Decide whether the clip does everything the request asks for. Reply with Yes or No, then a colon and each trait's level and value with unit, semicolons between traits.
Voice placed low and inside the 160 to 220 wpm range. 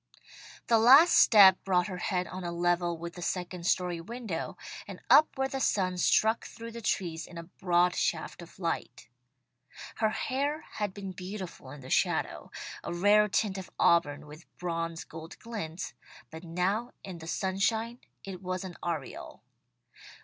No: medium, 185 Hz; average, 165 wpm